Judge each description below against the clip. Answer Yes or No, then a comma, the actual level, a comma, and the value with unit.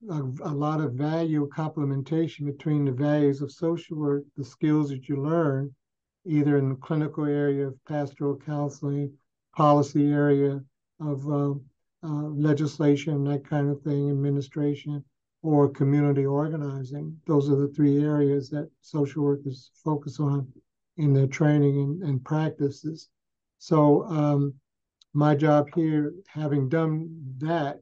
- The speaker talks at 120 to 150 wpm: Yes, slow, 135 wpm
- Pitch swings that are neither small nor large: No, narrow, 1.3 semitones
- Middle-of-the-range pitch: Yes, medium, 145 Hz